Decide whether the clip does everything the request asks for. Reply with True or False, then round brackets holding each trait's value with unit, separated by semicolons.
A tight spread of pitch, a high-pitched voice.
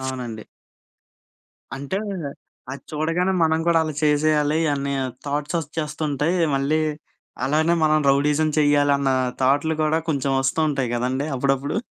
False (2.2 semitones; 145 Hz)